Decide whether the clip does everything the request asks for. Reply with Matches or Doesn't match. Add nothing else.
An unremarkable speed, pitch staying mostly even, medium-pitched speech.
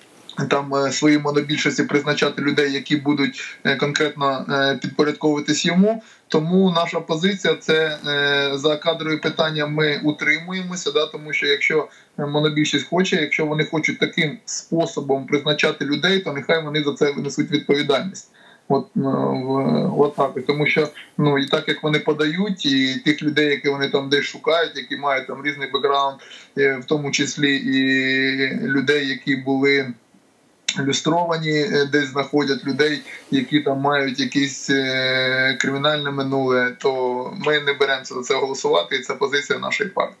Matches